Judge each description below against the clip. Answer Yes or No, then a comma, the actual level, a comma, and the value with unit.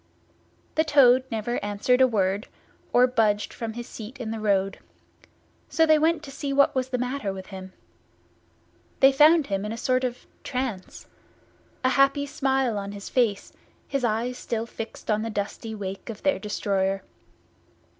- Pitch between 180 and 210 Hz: No, high, 235 Hz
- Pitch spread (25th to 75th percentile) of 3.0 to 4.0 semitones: No, average, 4.4 semitones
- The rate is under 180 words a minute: Yes, average, 170 wpm